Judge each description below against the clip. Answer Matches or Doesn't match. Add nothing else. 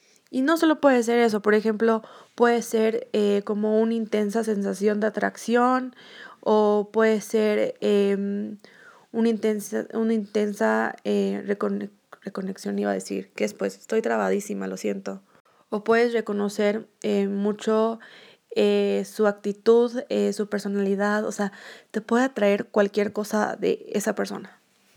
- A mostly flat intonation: Matches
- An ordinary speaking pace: Matches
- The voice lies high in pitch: Matches